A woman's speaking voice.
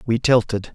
No: male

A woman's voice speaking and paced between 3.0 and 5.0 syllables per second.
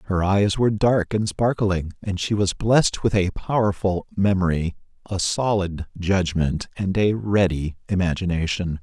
No: male; 4.5 syllables/s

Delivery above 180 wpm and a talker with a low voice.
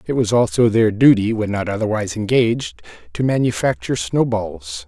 No: average, 160 wpm; low, 115 Hz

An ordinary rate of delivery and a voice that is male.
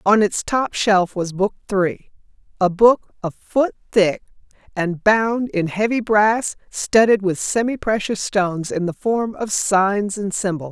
No: average, 160 wpm; female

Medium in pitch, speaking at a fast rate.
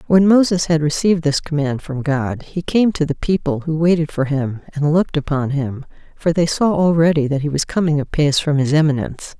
Yes: medium, 155 Hz; fast, 210 wpm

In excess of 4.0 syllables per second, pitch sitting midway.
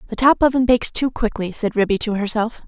No: 6.2 syllables/s; high, 225 Hz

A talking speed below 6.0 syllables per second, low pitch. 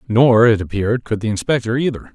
No: 6.1 syllables/s; low, 115 Hz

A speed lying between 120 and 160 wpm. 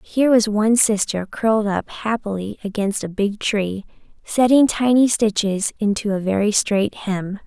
Yes: average, 155 wpm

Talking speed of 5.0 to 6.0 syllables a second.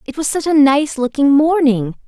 No: 4.8 syllables/s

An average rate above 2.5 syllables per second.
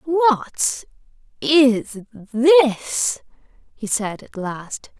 No: 1.9 syllables/s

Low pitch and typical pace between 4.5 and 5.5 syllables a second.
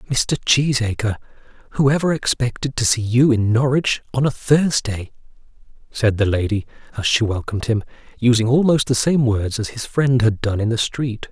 Yes: low, 120 Hz; 4.8 syllables/s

